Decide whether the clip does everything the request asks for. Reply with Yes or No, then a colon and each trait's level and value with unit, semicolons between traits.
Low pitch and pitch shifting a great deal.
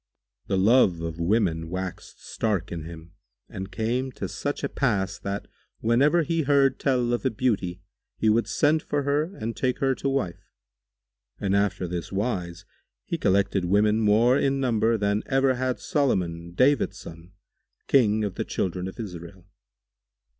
Yes: low, 105 Hz; wide, 5.9 semitones